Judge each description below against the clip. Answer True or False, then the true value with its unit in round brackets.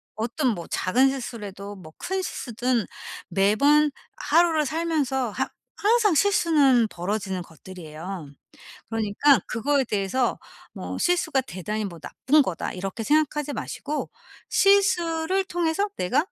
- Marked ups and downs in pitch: True (7.9 semitones)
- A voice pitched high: True (260 Hz)